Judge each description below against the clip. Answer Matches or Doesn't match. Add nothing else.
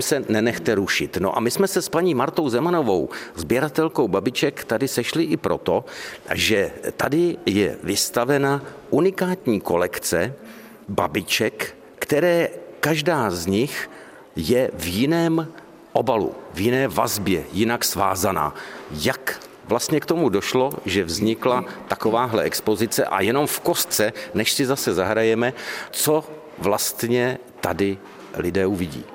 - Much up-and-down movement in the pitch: Matches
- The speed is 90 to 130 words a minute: Matches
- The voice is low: Matches